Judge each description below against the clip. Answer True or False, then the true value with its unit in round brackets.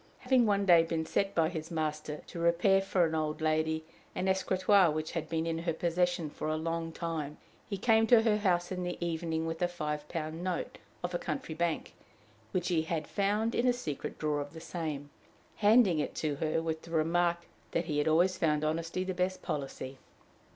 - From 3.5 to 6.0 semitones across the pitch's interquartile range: False (2.6 semitones)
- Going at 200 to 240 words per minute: True (205 wpm)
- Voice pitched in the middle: True (165 Hz)